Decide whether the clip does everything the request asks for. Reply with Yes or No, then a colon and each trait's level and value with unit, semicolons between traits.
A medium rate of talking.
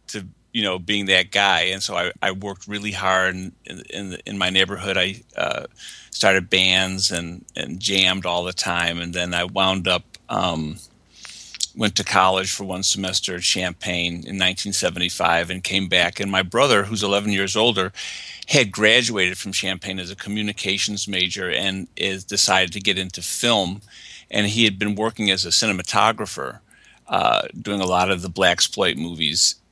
Yes: average, 170 wpm